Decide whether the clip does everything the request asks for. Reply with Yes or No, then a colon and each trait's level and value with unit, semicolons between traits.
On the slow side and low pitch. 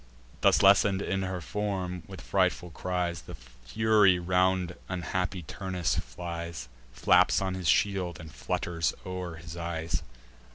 Yes: slow, 130 wpm; very low, 90 Hz